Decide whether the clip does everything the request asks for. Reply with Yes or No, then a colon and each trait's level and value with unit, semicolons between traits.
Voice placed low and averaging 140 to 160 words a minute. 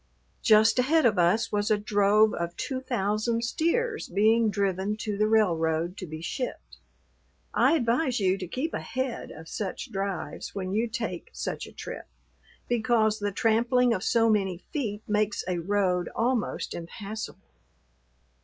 No: high, 215 Hz; average, 150 wpm